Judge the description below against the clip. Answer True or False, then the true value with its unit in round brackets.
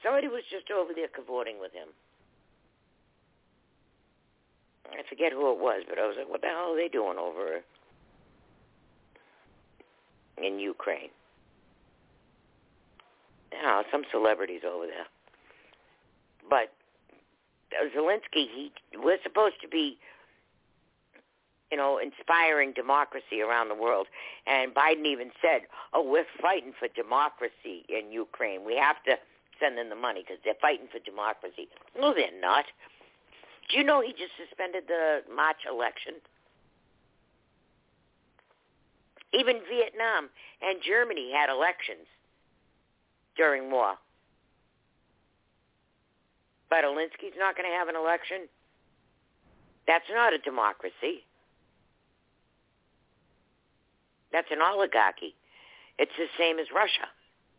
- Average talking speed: False (115 wpm)